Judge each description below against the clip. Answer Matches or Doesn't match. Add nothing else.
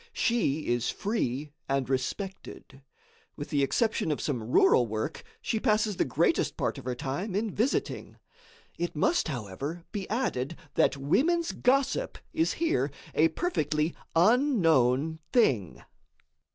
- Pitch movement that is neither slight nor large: Doesn't match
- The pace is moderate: Doesn't match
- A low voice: Doesn't match